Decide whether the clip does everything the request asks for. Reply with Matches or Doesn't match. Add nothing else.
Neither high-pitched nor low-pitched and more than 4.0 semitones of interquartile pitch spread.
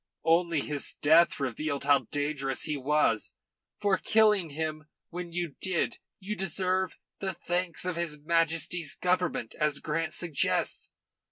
Doesn't match